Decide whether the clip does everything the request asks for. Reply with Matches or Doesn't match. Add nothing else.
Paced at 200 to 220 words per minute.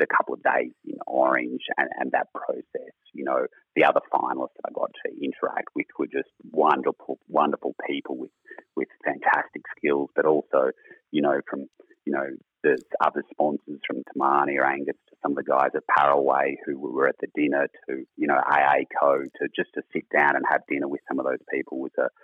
Matches